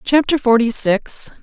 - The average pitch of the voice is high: Yes, high, 245 Hz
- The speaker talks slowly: Yes, slow, 125 wpm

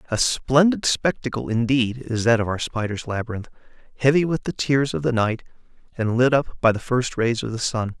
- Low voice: Yes, low, 120 Hz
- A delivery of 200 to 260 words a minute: Yes, fast, 205 wpm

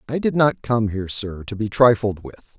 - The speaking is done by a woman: No, male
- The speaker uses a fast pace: Yes, fast, 230 wpm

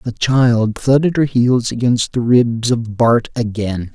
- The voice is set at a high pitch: No, low, 120 Hz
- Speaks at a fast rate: No, average, 165 wpm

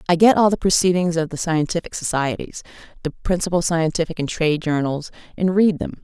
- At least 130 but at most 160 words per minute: No, average, 180 wpm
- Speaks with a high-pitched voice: No, medium, 165 Hz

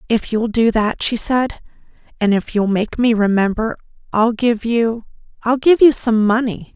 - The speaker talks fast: No, average, 170 wpm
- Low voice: No, high, 225 Hz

